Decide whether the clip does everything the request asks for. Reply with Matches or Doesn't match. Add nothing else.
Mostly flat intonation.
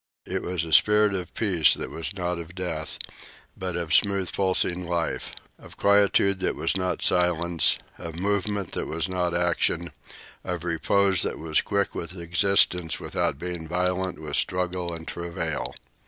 Matches